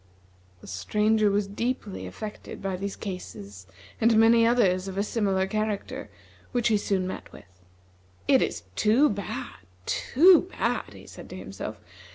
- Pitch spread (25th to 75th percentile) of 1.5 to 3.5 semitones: Yes, average, 3.1 semitones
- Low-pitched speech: No, high, 205 Hz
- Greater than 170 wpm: No, average, 150 wpm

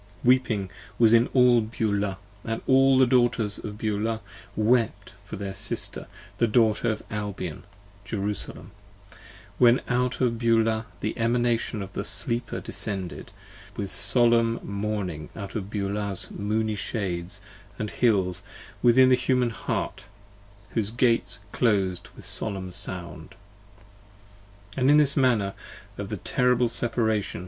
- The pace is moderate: No, slow, 130 wpm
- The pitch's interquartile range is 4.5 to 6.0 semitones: No, average, 3.1 semitones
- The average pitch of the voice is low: Yes, low, 110 Hz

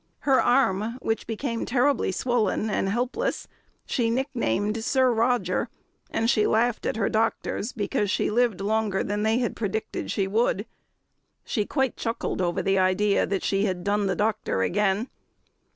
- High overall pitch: Yes, high, 220 Hz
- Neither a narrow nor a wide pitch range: Yes, average, 3.3 semitones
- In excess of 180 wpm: No, average, 155 wpm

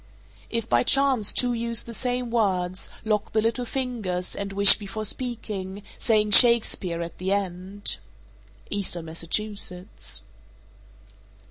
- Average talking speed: No, slow, 125 wpm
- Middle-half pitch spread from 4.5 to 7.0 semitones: No, average, 3.9 semitones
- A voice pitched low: No, high, 210 Hz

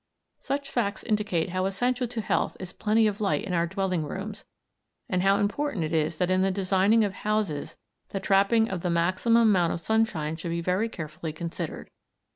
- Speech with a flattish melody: No, average, 3.9 semitones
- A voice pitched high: Yes, high, 195 Hz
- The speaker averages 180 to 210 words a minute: Yes, average, 190 wpm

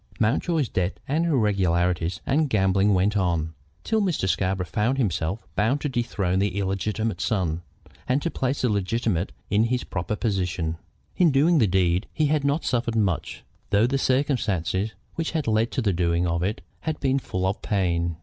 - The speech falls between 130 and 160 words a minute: No, average, 175 wpm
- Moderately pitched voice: No, low, 105 Hz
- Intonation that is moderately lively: No, wide, 6.1 semitones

